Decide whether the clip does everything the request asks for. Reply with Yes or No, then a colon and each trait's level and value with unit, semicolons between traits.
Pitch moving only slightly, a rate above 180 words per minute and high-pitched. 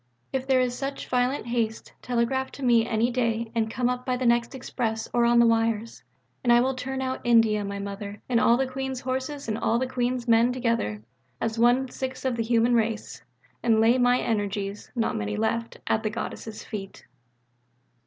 Yes: narrow, 2.2 semitones; average, 195 wpm; high, 235 Hz